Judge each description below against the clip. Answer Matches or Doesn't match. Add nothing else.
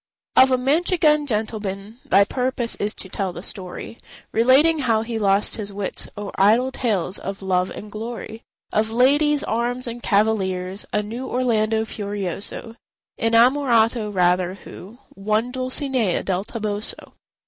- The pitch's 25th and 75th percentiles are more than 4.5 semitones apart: Doesn't match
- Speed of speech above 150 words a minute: Doesn't match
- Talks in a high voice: Matches